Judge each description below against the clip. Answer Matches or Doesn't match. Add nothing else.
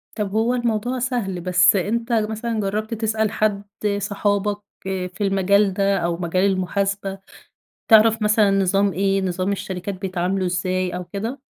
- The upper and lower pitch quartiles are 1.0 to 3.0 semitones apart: Matches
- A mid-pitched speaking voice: Doesn't match